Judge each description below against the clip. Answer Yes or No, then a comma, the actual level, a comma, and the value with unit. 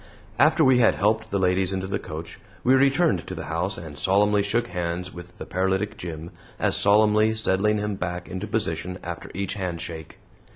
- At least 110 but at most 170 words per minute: No, average, 180 wpm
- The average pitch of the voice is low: Yes, very low, 95 Hz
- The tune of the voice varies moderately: Yes, average, 3.4 semitones